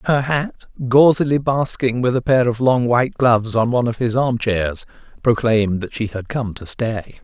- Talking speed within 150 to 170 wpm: No, average, 200 wpm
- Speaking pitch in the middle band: No, low, 120 Hz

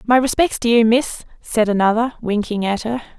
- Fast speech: No, average, 190 wpm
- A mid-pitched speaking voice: No, high, 230 Hz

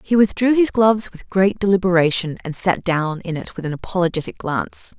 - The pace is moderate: Yes, average, 190 wpm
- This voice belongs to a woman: Yes, female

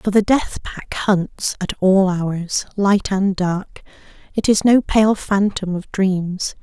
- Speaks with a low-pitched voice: No, high, 195 Hz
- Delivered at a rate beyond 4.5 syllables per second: No, 3.3 syllables/s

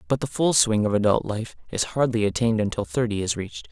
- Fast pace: Yes, fast, 225 wpm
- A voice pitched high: No, low, 115 Hz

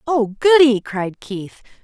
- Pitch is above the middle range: Yes, high, 245 Hz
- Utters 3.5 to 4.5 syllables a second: No, 3.3 syllables/s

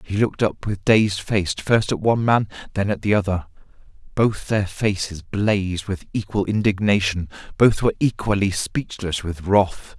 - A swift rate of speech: No, average, 160 wpm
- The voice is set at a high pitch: No, low, 100 Hz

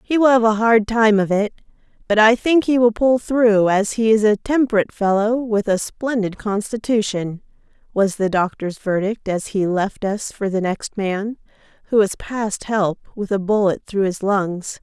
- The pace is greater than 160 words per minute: Yes, average, 190 wpm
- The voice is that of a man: No, female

